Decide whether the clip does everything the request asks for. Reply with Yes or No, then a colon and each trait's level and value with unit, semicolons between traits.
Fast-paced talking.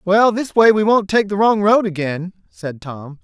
Yes: fast, 220 wpm